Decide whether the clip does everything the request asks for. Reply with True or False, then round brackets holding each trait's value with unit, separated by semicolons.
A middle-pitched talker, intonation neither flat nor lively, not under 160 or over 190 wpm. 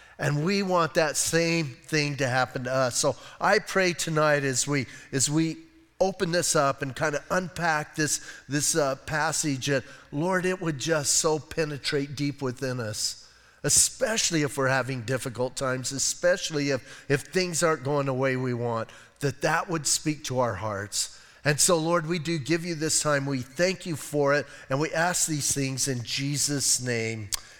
True (145 Hz; 3.5 semitones; 185 wpm)